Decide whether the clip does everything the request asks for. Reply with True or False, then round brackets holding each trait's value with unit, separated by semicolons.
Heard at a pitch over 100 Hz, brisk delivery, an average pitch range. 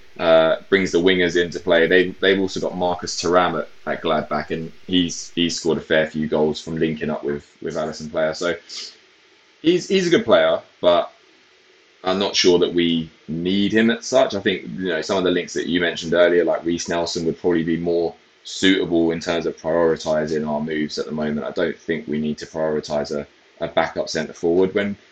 False (85 Hz; 210 wpm; 3.0 semitones)